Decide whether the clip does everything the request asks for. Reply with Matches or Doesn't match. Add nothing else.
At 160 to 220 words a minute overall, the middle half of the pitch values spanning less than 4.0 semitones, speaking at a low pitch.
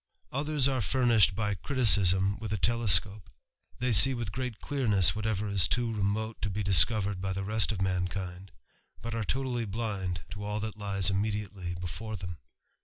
Matches